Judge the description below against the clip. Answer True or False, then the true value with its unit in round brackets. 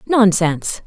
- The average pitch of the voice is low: False (200 Hz)